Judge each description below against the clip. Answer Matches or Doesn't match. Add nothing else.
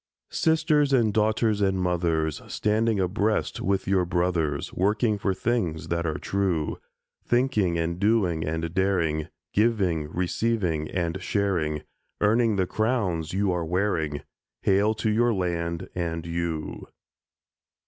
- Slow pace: Matches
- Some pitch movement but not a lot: Matches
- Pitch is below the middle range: Matches